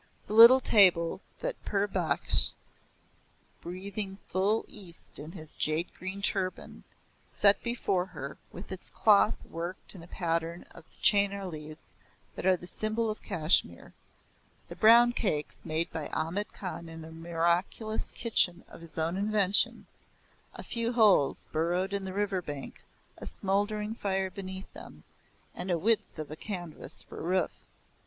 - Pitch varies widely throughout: No, average, 3.7 semitones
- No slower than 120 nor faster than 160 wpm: Yes, average, 150 wpm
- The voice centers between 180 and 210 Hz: Yes, high, 190 Hz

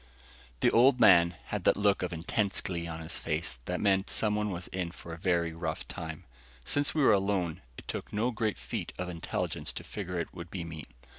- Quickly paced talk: Yes, fast, 210 wpm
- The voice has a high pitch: No, very low, 90 Hz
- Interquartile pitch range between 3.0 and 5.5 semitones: Yes, average, 3.5 semitones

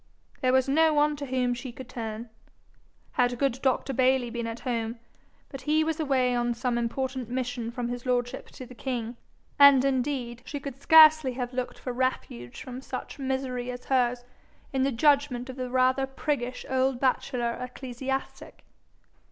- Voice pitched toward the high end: Yes, very high, 255 Hz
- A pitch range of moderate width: No, narrow, 1.8 semitones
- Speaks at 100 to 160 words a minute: No, average, 170 wpm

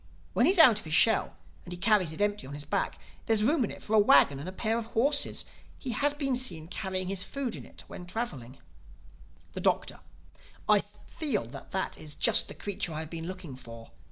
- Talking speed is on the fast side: Yes, fast, 230 wpm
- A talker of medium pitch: No, high, 195 Hz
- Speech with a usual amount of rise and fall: No, wide, 6.6 semitones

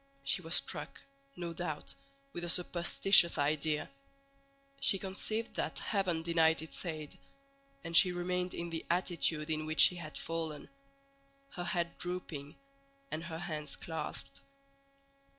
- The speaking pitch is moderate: Yes, medium, 170 Hz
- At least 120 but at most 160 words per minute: Yes, slow, 135 wpm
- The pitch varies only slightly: Yes, narrow, 2.2 semitones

